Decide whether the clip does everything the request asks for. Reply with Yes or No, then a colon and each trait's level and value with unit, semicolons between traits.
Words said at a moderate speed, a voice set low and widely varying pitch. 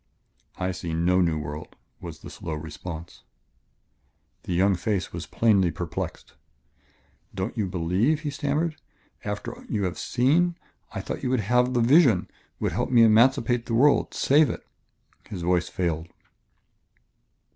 Yes: average, 145 wpm; low, 100 Hz; wide, 6.5 semitones